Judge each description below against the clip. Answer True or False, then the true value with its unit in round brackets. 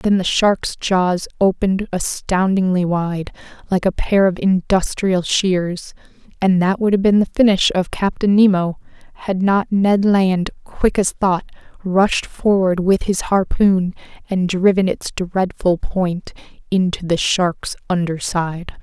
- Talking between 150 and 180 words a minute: False (140 wpm)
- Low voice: False (190 Hz)